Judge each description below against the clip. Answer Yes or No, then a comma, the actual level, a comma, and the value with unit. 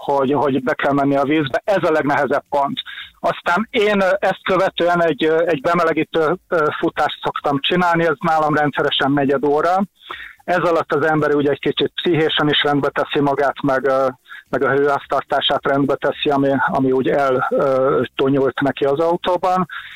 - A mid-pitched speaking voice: Yes, medium, 150 Hz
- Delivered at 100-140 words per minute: No, fast, 155 wpm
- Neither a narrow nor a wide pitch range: Yes, average, 3.5 semitones